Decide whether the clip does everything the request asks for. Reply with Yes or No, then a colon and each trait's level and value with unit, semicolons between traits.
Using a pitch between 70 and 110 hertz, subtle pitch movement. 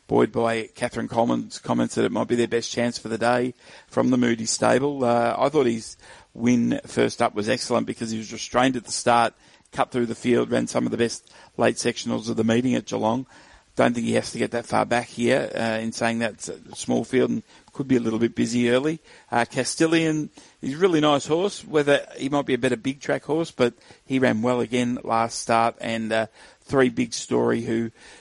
No: low, 120 Hz; narrow, 1.9 semitones